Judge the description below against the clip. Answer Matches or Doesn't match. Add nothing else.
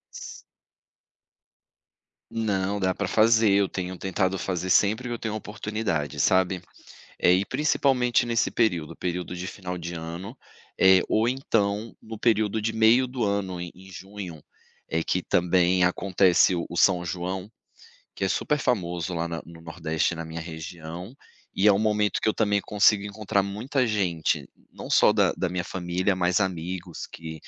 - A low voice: Matches